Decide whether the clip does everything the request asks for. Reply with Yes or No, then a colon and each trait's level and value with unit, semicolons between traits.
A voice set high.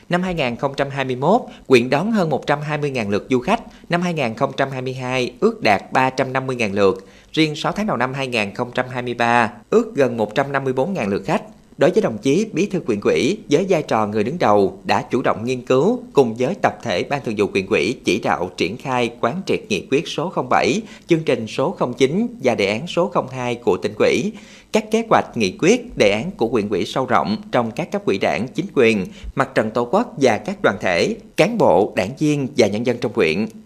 No: low, 135 Hz